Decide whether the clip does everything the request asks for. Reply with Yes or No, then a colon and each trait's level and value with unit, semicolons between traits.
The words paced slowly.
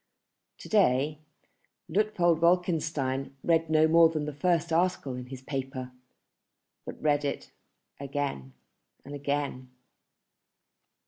Yes: slow, 110 wpm